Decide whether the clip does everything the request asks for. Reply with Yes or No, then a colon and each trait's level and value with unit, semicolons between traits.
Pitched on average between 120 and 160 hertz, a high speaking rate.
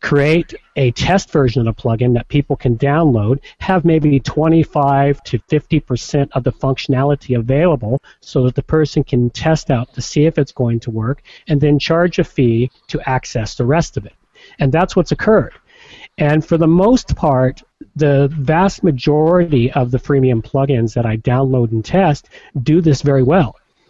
No: medium, 140 Hz; average, 175 wpm